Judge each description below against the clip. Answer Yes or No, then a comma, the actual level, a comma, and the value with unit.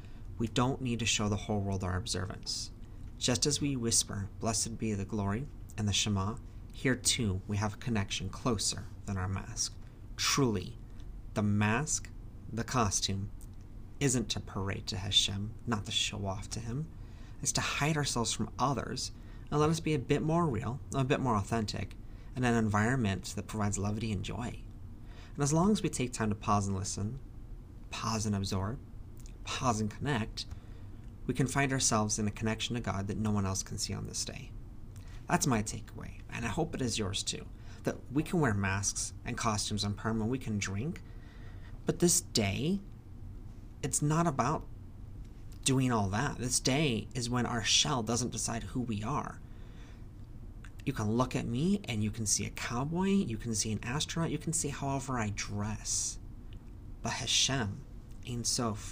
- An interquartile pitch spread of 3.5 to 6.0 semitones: No, average, 2.8 semitones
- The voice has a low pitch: Yes, low, 110 Hz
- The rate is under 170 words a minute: No, average, 180 wpm